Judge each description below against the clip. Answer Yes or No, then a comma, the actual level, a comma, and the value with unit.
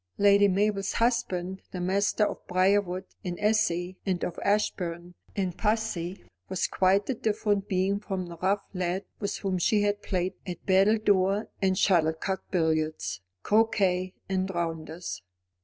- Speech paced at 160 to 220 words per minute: No, average, 140 wpm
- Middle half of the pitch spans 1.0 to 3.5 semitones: Yes, narrow, 2.4 semitones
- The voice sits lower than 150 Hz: No, high, 190 Hz